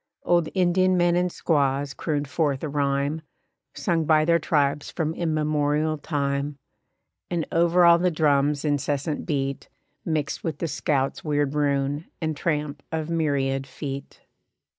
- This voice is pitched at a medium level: Yes, medium, 150 Hz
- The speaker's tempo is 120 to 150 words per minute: Yes, average, 140 wpm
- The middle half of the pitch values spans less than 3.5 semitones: Yes, narrow, 2.6 semitones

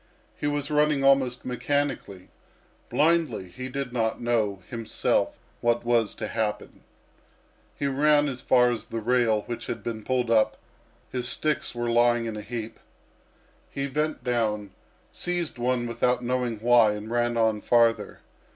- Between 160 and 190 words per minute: No, average, 150 wpm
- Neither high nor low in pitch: No, low, 120 Hz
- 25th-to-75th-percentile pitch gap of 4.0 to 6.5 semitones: No, average, 2.8 semitones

